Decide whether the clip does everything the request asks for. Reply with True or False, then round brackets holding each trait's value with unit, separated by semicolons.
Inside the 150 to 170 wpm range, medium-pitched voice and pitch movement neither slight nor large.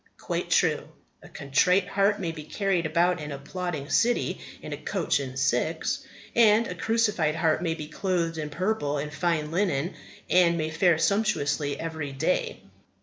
True (160 wpm; 165 Hz; 3.8 semitones)